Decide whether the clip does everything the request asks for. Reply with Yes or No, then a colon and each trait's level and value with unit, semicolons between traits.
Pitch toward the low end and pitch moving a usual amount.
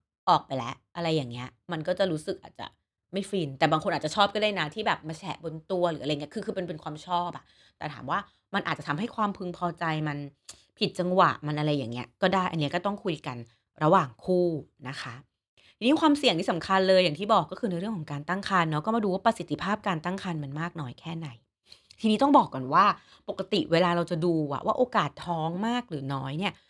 No: medium, 175 Hz; average, 4.4 semitones